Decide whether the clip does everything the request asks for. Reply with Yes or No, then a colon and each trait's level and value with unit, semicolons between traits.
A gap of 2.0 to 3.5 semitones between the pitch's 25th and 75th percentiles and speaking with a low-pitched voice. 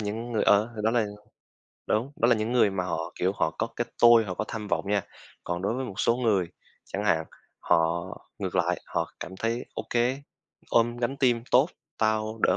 Yes: average, 3.0 semitones; low, 110 Hz